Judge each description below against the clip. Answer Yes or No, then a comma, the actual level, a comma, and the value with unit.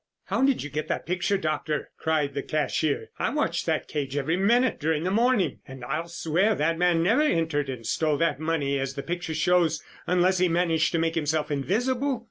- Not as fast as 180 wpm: No, average, 200 wpm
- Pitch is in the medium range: Yes, medium, 165 Hz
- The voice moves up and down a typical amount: Yes, average, 3.4 semitones